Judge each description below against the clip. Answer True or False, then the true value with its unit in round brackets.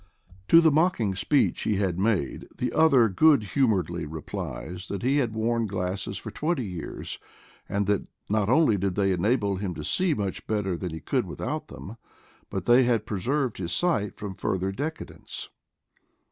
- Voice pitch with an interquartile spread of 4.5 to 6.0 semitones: True (5.0 semitones)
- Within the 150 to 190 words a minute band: True (170 wpm)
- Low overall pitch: True (105 Hz)